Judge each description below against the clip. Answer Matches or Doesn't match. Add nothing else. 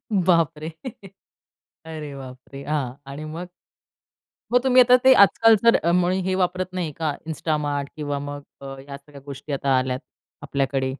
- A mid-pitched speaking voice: Matches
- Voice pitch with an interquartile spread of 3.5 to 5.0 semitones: Matches